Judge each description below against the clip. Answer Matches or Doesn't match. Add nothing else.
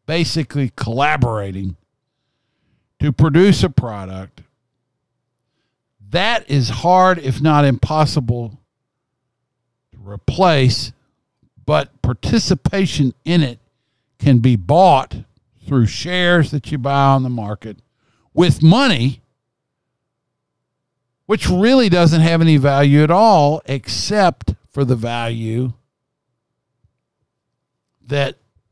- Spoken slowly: Matches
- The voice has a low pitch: Matches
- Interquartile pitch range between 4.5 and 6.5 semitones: Doesn't match